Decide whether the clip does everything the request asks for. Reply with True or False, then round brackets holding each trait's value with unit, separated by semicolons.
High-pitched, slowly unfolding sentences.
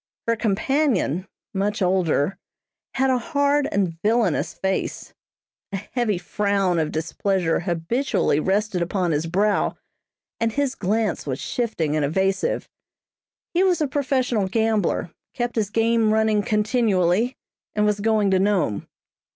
True (205 Hz; 130 wpm)